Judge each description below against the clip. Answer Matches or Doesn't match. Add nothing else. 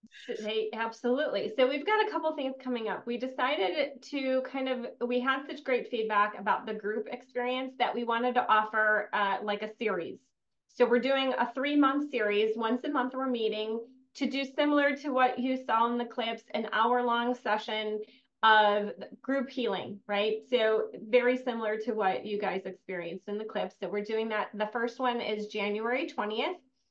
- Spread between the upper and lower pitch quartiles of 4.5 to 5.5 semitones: Doesn't match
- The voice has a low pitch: Doesn't match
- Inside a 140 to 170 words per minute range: Doesn't match